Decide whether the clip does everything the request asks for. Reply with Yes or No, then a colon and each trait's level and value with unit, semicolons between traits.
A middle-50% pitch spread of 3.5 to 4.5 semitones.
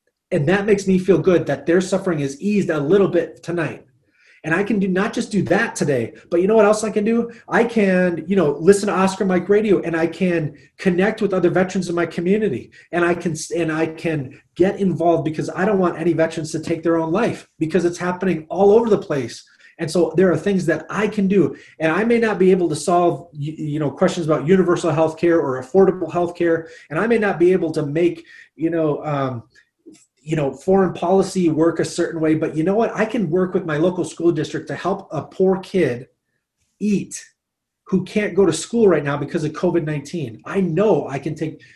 No: average, 3.1 semitones